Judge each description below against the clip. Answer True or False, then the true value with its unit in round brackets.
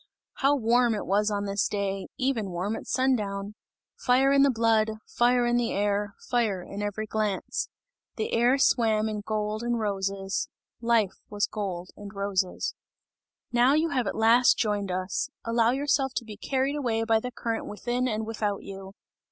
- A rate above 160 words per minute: True (170 wpm)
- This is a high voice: True (220 Hz)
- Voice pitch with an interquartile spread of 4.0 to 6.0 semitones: False (3.1 semitones)